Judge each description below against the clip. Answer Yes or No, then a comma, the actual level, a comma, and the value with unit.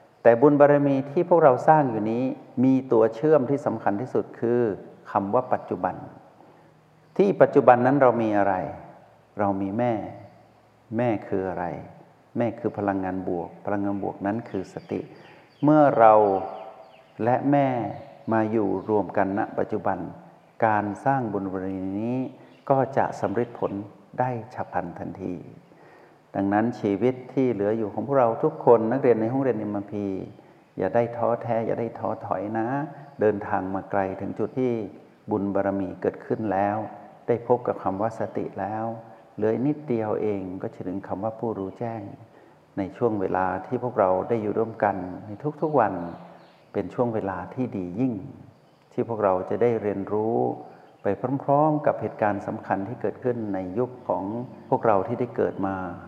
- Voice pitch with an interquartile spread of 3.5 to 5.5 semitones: Yes, average, 3.9 semitones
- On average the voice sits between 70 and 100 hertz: No, low, 110 Hz